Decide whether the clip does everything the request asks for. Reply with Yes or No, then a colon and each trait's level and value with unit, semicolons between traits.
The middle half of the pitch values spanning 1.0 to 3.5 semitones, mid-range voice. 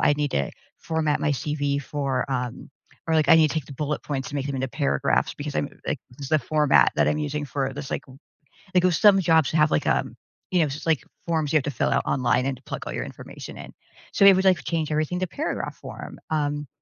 Yes: narrow, 2.5 semitones; medium, 150 Hz